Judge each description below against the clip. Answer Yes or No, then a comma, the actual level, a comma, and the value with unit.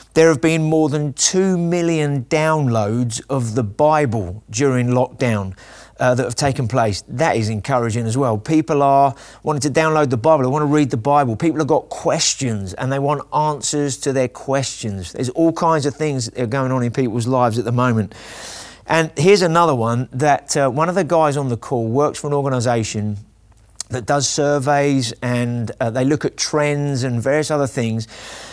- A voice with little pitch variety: No, average, 3.9 semitones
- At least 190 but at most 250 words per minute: Yes, average, 195 wpm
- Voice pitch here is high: No, low, 135 Hz